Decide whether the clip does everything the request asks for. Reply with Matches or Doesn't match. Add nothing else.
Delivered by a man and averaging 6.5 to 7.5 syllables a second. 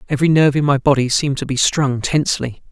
Matches